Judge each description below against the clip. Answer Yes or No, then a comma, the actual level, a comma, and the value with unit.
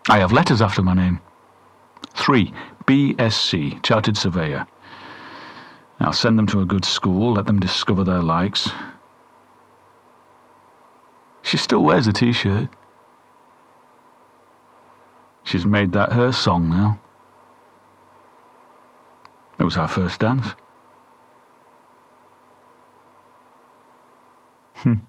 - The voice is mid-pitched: No, low, 100 Hz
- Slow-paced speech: Yes, slow, 95 wpm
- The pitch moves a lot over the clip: No, average, 3.5 semitones